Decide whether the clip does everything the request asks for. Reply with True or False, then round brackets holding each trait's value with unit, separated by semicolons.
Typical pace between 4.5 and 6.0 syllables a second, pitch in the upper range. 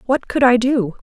True (4.7 syllables/s; 245 Hz)